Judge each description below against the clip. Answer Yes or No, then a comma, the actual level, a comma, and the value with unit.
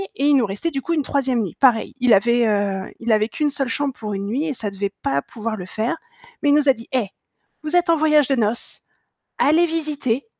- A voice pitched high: Yes, very high, 250 Hz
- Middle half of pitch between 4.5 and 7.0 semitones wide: Yes, wide, 5.4 semitones